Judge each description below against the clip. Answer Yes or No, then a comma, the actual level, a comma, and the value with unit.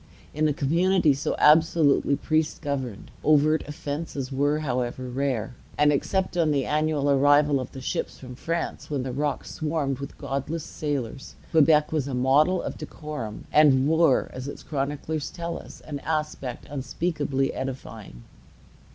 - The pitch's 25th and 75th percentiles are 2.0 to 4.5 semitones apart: Yes, narrow, 2.5 semitones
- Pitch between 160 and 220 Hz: No, medium, 145 Hz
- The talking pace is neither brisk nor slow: Yes, average, 150 wpm